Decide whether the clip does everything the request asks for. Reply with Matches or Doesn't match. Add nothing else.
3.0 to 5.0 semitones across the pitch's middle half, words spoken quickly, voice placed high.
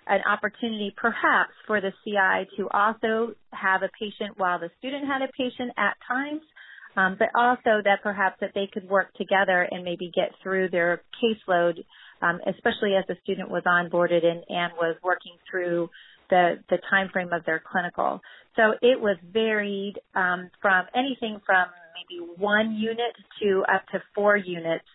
Doesn't match